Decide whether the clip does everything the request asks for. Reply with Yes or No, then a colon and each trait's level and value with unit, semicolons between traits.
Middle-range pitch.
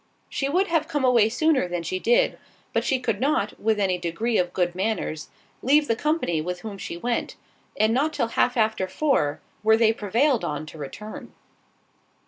No: high, 220 Hz